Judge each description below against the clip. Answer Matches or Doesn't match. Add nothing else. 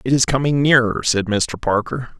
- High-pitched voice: Doesn't match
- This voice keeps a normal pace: Matches